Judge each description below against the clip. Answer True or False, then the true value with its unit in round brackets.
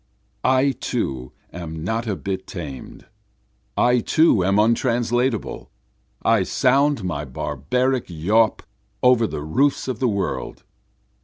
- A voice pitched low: True (110 Hz)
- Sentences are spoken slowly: True (115 wpm)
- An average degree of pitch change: False (6.6 semitones)